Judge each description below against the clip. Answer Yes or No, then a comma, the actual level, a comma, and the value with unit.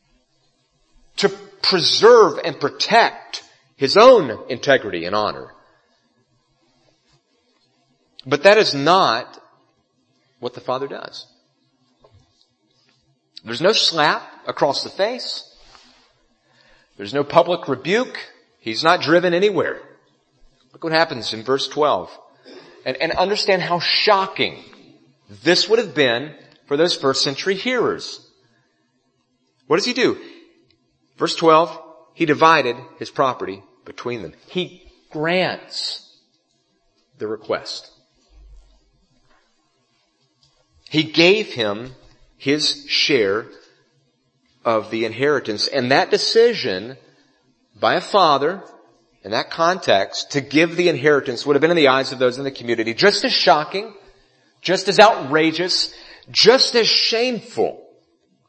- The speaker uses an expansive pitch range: Yes, wide, 7.3 semitones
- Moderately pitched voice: Yes, medium, 165 Hz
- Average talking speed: No, slow, 110 wpm